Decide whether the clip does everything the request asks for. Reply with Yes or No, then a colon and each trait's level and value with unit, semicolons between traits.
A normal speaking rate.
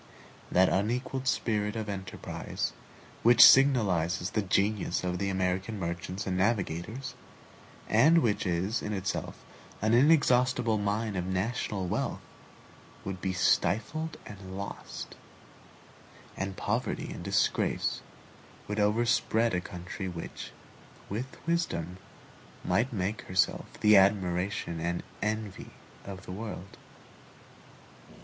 No: slow, 110 wpm